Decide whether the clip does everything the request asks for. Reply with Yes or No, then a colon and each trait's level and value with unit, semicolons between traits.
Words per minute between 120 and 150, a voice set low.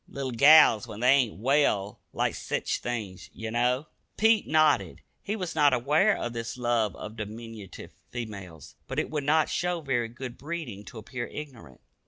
No: average, 170 wpm; low, 120 Hz